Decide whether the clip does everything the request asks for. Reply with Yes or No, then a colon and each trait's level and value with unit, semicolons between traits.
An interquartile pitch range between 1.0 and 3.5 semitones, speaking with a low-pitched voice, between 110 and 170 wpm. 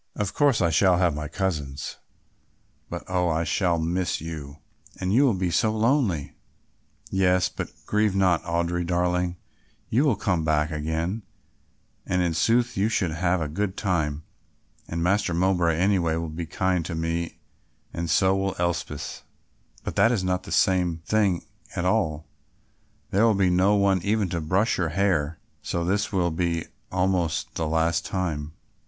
Yes: average, 2.8 semitones; very low, 90 Hz; average, 165 wpm